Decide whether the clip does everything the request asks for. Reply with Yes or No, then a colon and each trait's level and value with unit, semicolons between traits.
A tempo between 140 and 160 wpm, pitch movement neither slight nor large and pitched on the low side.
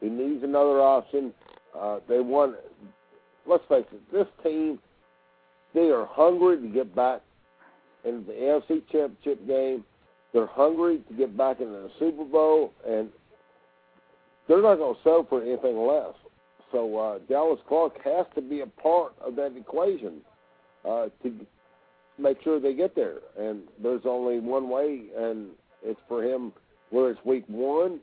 No: average, 155 wpm; wide, 6.2 semitones; low, 130 Hz